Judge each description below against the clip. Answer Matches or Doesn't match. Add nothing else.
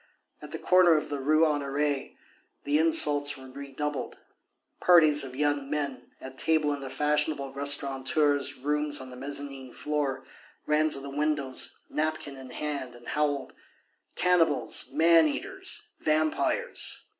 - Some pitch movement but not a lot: Doesn't match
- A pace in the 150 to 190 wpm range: Doesn't match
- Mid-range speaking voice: Matches